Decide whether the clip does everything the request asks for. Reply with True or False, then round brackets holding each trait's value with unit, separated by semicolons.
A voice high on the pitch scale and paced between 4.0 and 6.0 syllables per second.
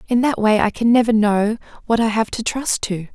True (220 Hz; 5.3 syllables/s)